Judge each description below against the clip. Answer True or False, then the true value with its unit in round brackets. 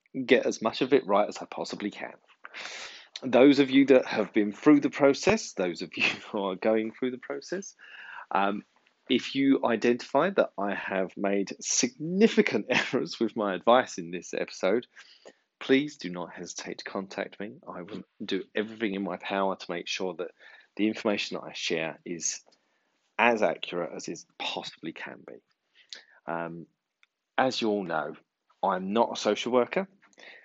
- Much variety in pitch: True (6.1 semitones)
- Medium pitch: False (110 Hz)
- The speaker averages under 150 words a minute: False (170 wpm)